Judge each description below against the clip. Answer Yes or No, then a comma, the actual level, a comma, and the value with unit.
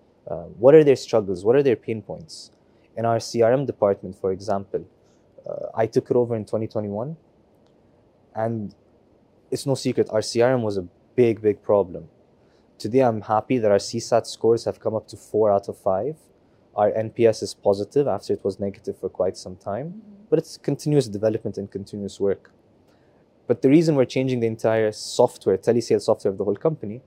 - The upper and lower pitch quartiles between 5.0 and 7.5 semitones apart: No, average, 3.7 semitones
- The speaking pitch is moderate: No, low, 115 Hz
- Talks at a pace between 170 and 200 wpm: Yes, average, 180 wpm